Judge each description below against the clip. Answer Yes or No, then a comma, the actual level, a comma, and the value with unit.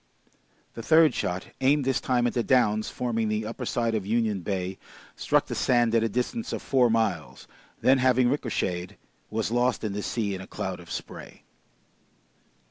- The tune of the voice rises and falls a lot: No, average, 2.9 semitones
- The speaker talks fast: No, average, 180 wpm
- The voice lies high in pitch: No, low, 115 Hz